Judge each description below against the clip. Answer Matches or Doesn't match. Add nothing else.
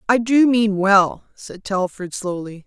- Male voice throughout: Doesn't match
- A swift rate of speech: Doesn't match